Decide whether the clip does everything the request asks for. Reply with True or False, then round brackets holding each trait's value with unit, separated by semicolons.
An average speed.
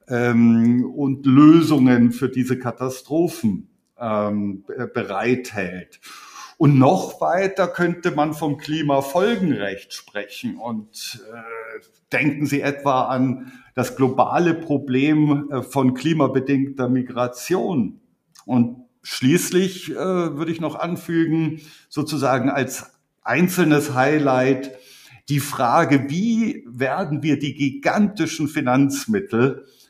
False (90 wpm)